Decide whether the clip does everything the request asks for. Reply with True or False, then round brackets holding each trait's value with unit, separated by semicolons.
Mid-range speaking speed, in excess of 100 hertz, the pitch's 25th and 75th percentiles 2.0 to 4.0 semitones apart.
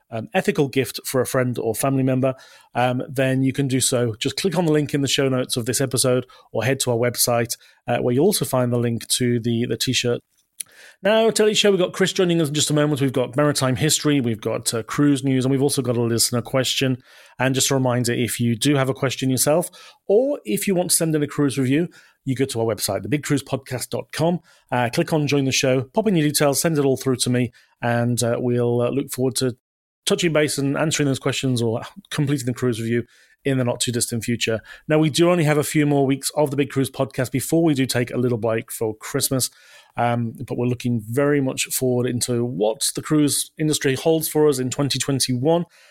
False (235 wpm; 135 Hz; 3.3 semitones)